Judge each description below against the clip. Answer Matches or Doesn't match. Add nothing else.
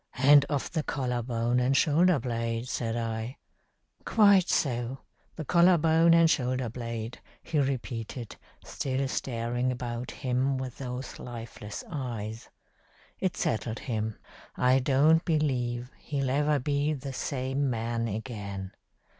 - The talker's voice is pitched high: Doesn't match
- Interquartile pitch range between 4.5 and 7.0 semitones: Doesn't match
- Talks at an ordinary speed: Doesn't match